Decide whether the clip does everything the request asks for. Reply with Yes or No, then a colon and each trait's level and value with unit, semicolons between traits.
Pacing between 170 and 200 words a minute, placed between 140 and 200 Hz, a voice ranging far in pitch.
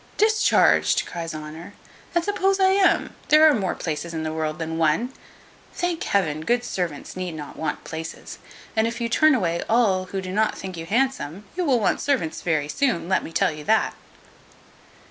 Yes: average, 185 wpm; medium, 185 Hz; wide, 7.8 semitones